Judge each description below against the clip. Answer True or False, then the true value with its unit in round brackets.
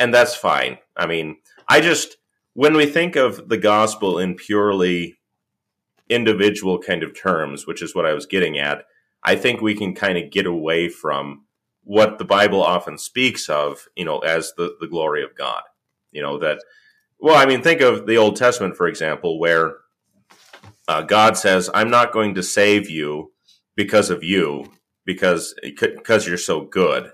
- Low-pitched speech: True (105 Hz)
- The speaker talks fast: False (180 wpm)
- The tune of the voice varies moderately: False (6.2 semitones)